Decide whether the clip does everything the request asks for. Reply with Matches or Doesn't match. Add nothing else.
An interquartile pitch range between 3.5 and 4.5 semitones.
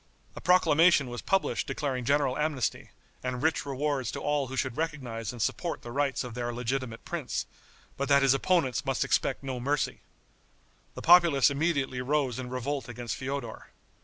Doesn't match